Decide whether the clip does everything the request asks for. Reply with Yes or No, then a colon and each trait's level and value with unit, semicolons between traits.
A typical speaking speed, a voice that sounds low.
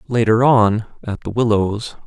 Yes: average, 145 wpm; low, 110 Hz